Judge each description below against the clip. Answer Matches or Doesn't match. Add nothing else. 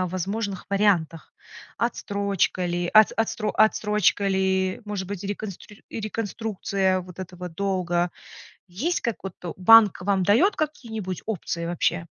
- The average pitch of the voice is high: Matches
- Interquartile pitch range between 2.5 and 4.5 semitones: Matches